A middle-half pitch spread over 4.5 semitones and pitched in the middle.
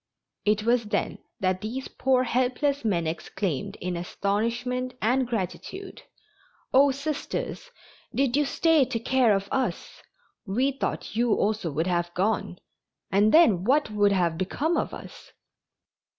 No: average, 5.3 semitones; high, 230 Hz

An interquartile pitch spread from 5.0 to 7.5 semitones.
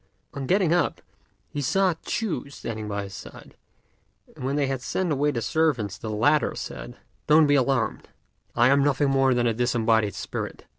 No: average, 4.3 semitones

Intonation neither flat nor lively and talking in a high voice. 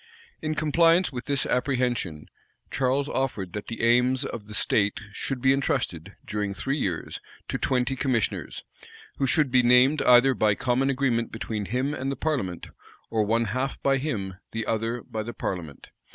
No: average, 4.0 semitones; low, 125 Hz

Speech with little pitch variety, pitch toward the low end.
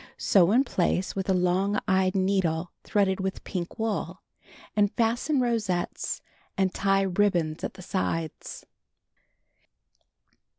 No: narrow, 2.3 semitones; high, 190 Hz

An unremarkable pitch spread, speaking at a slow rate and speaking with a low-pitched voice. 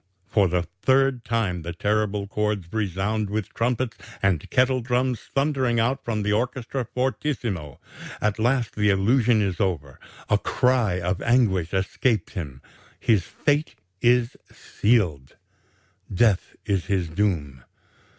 Yes: average, 4.7 semitones; slow, 130 wpm; low, 105 Hz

